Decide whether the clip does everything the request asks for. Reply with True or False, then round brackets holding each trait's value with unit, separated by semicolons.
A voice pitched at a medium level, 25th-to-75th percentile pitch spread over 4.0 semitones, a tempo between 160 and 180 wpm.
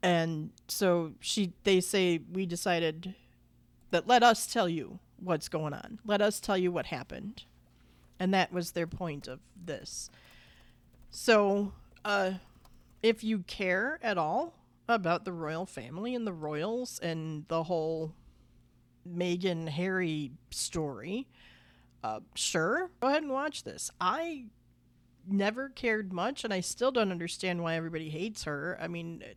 False (180 Hz; 4.5 semitones; 145 wpm)